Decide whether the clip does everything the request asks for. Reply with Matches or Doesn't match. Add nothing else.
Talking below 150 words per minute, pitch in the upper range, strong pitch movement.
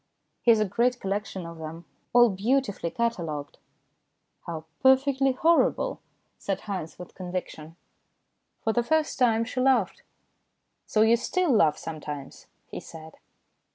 Matches